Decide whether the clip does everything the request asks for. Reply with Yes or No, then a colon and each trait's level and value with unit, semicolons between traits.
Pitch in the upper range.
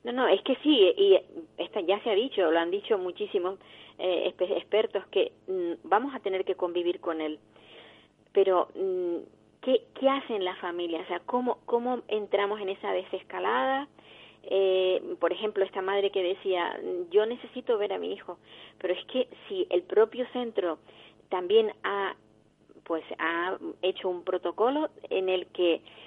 Yes: high, 205 Hz